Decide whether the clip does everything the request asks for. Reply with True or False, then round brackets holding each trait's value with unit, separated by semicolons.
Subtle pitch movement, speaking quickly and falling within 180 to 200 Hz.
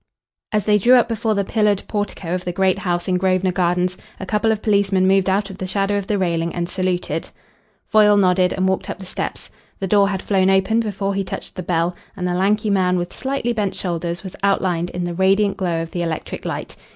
True (2.1 semitones; 225 wpm; 190 Hz)